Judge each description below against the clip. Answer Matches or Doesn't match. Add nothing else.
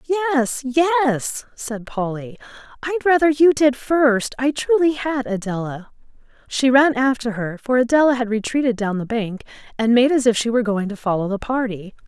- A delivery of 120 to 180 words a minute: Matches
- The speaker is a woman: Matches